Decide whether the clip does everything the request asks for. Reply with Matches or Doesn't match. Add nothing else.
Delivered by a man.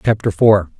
Matches